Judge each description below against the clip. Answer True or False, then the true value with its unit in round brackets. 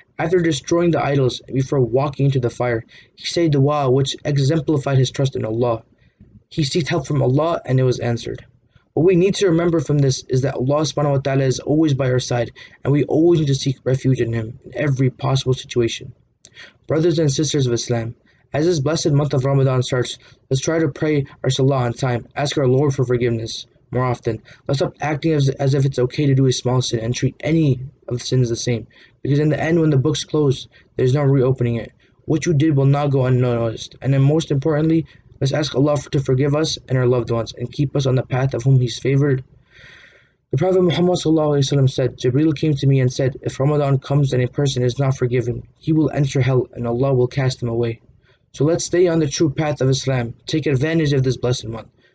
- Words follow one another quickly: True (220 wpm)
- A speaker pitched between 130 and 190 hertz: True (135 Hz)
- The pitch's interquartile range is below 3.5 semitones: True (2.9 semitones)